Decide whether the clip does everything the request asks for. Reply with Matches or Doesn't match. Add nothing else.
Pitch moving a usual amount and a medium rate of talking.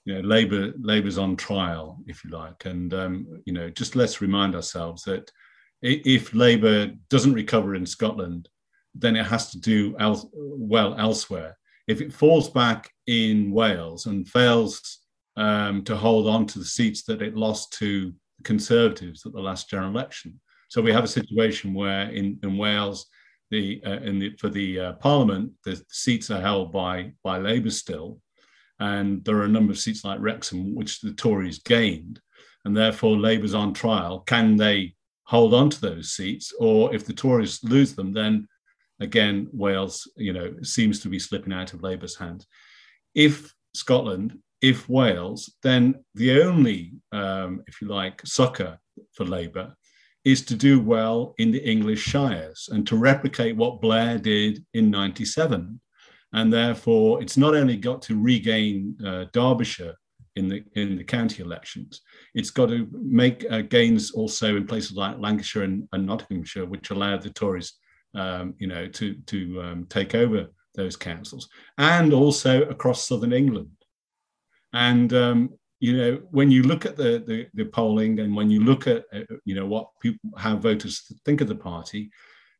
Matches